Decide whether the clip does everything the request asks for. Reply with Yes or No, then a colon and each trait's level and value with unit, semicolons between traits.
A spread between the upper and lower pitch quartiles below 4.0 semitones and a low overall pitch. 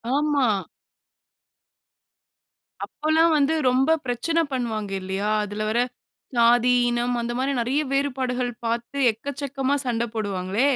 No: average, 3.5 semitones; high, 245 Hz